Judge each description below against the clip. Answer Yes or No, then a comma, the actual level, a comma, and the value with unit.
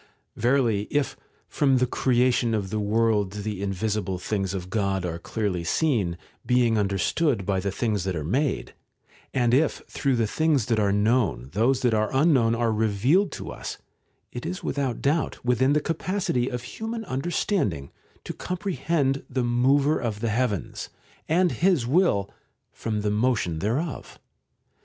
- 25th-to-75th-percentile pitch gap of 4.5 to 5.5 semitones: Yes, average, 5.2 semitones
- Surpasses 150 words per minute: Yes, average, 165 wpm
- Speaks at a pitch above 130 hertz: No, low, 120 Hz